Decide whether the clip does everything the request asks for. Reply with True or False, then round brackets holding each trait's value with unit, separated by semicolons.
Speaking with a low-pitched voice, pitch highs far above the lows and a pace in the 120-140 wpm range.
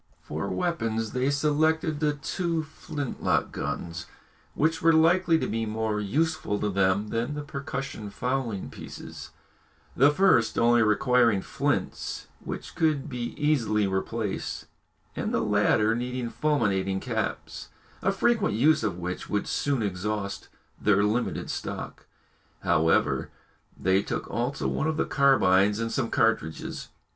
True (120 Hz; 6.3 semitones; 135 wpm)